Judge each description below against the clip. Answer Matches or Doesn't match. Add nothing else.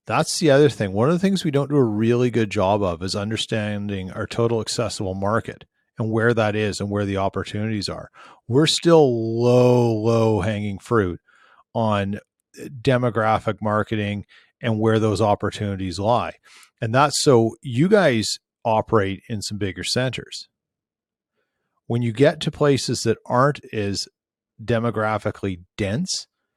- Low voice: Matches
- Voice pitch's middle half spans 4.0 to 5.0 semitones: Doesn't match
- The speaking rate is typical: Matches